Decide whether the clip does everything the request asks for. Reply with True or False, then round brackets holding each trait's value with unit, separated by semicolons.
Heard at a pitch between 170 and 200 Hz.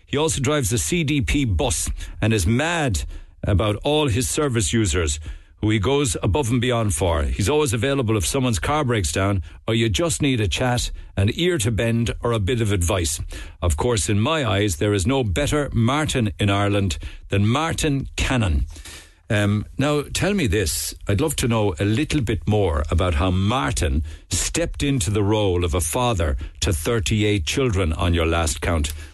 False (105 Hz)